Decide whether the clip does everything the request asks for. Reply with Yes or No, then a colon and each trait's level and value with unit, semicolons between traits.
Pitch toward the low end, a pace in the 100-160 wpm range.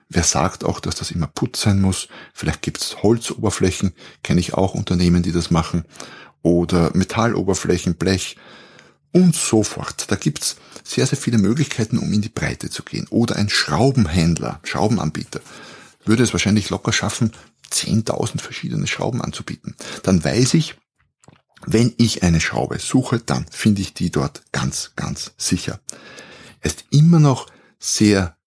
Yes: low, 105 Hz; average, 155 wpm